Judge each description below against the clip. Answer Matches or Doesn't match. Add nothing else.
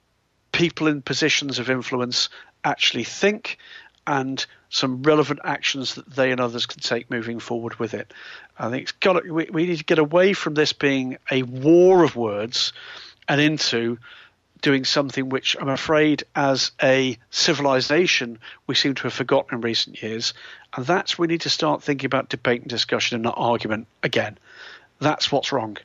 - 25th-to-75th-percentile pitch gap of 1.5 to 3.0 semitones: Doesn't match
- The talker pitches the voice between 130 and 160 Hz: Matches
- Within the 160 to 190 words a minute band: Matches